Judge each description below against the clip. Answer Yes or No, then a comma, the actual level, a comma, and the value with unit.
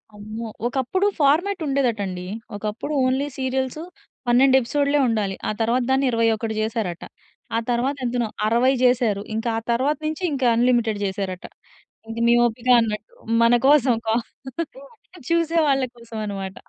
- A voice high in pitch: Yes, high, 240 Hz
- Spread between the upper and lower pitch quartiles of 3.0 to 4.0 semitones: Yes, average, 3.5 semitones